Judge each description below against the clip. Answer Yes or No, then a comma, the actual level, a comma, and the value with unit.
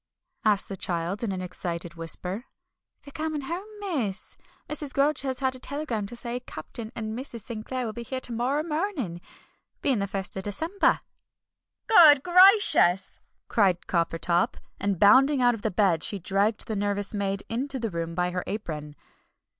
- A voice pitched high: Yes, high, 220 Hz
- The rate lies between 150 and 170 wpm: Yes, average, 165 wpm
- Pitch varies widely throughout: Yes, wide, 6.1 semitones